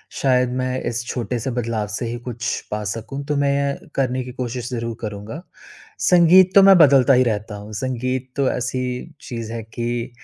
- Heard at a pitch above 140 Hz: No, low, 125 Hz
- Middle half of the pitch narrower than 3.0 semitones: Yes, narrow, 2.5 semitones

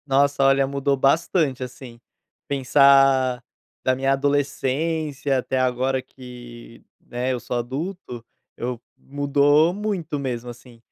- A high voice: No, low, 135 Hz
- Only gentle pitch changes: Yes, narrow, 2.1 semitones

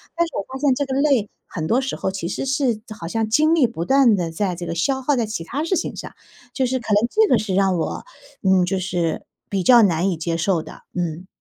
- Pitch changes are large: Yes, wide, 7.0 semitones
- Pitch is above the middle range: Yes, high, 210 Hz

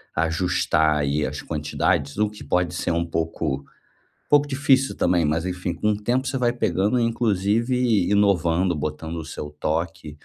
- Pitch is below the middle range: Yes, very low, 90 Hz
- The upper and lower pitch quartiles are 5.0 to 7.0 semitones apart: Yes, wide, 5.4 semitones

